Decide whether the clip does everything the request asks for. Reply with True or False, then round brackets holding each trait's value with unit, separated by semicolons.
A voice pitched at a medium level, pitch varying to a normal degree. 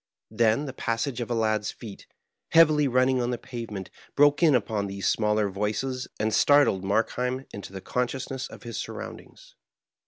False (120 Hz; 3.7 semitones)